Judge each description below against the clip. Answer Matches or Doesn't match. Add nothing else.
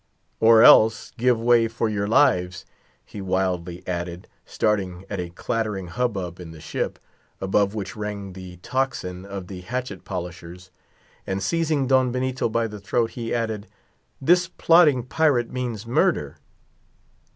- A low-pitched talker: Matches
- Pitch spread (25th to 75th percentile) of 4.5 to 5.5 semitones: Matches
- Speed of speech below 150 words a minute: Matches